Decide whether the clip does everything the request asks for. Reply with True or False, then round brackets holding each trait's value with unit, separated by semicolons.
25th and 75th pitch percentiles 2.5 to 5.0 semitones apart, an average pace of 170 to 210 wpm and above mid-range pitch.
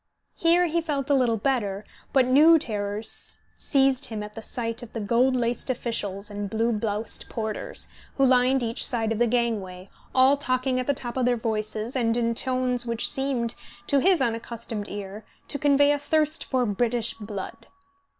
True (3.4 semitones; 180 wpm; 240 Hz)